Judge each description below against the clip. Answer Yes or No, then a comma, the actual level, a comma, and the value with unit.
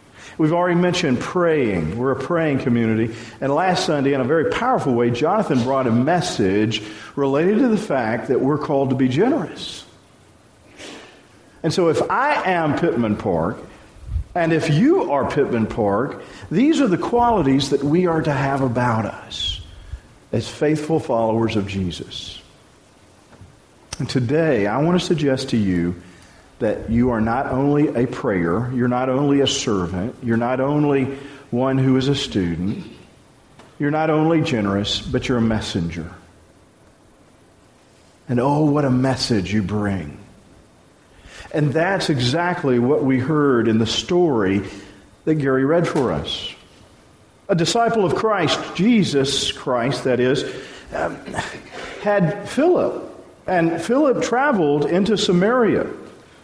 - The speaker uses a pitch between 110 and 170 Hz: Yes, low, 135 Hz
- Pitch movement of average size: No, wide, 5.9 semitones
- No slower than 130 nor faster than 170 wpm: Yes, average, 140 wpm